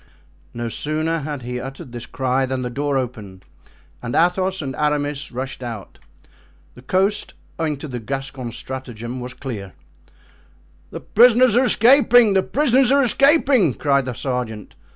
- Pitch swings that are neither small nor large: No, wide, 7.3 semitones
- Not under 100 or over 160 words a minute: Yes, average, 150 wpm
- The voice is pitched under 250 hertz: Yes, low, 135 Hz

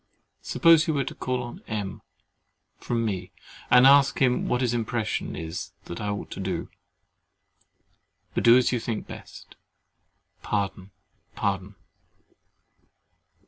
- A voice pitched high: No, low, 115 Hz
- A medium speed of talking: No, slow, 130 wpm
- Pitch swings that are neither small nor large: Yes, average, 4.3 semitones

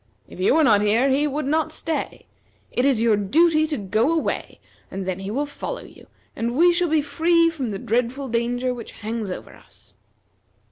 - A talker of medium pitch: No, very high, 255 Hz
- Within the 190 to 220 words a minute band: Yes, average, 195 wpm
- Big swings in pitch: Yes, wide, 5.9 semitones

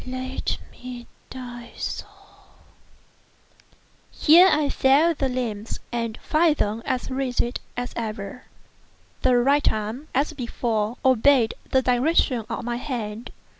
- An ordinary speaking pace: No, slow, 120 wpm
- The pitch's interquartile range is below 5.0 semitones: Yes, average, 2.7 semitones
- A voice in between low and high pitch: No, very high, 250 Hz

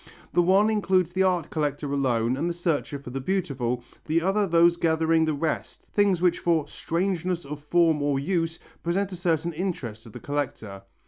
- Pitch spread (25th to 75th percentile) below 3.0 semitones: No, average, 3.9 semitones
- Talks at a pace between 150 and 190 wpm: Yes, average, 185 wpm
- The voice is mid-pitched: Yes, medium, 165 Hz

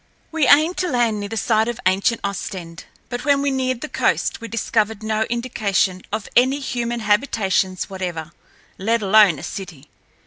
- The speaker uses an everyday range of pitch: Yes, average, 4.0 semitones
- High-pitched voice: Yes, high, 220 Hz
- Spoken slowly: No, average, 170 wpm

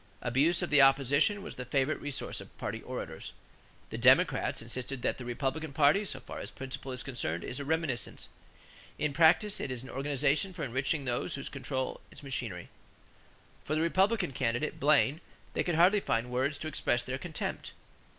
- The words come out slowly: No, average, 180 wpm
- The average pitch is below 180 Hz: Yes, medium, 140 Hz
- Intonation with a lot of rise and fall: No, average, 3.7 semitones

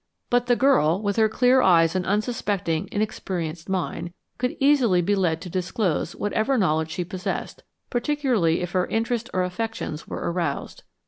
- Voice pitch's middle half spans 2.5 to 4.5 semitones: No, average, 5.2 semitones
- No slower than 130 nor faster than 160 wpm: Yes, average, 155 wpm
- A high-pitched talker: Yes, high, 195 Hz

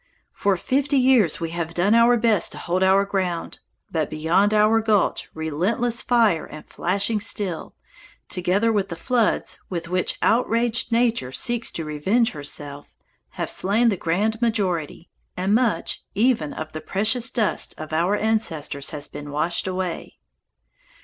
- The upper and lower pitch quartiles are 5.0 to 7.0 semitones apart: Yes, wide, 5.4 semitones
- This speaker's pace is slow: No, average, 150 wpm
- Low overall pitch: No, high, 195 Hz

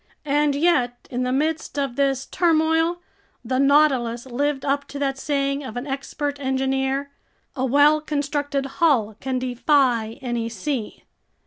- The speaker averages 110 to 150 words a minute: Yes, average, 140 wpm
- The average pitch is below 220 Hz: No, very high, 275 Hz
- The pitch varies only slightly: Yes, narrow, 2.3 semitones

